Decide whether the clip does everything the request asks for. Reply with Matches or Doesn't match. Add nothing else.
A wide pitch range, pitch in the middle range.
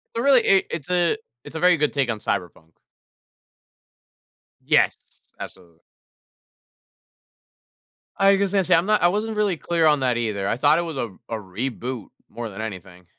Matches